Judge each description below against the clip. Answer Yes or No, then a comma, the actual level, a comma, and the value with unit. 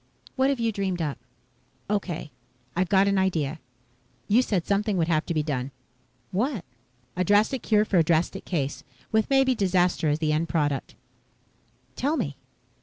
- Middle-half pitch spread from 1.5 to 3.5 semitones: No, average, 4.8 semitones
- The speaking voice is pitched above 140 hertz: Yes, medium, 185 Hz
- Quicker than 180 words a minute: No, average, 165 wpm